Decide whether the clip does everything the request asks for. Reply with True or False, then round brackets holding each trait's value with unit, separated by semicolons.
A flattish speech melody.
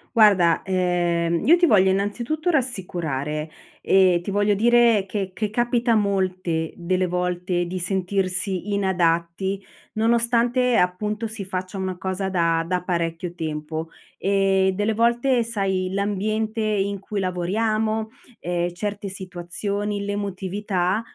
False (3.1 semitones)